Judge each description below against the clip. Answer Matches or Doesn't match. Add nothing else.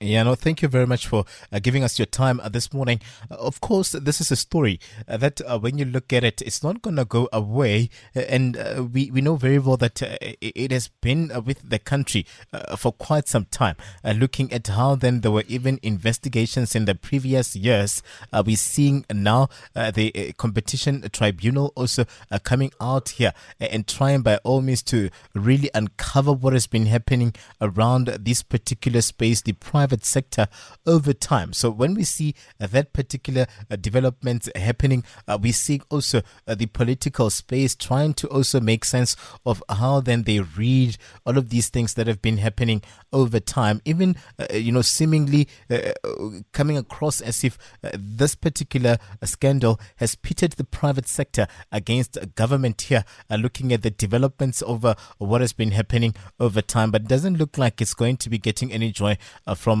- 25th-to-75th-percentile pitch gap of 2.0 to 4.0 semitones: Matches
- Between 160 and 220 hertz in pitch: Doesn't match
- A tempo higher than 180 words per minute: Matches